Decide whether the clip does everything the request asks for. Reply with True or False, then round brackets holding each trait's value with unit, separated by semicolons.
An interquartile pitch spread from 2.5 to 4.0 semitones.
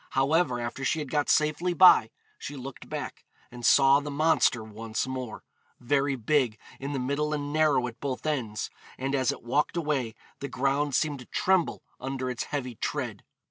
True (3.0 semitones)